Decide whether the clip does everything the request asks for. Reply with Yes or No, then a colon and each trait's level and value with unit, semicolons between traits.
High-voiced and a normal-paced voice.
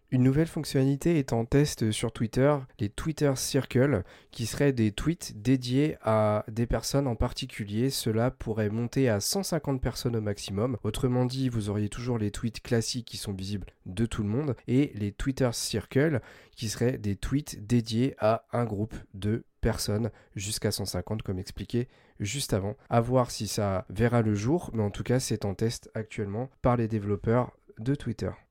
No: low, 115 Hz; average, 175 wpm